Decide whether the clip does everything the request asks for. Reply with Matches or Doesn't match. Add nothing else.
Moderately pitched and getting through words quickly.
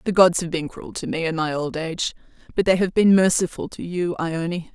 Matches